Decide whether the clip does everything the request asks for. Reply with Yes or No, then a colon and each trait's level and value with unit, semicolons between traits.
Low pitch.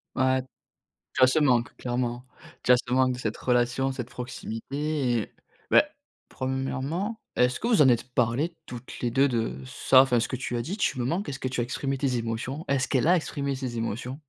Yes: low, 130 Hz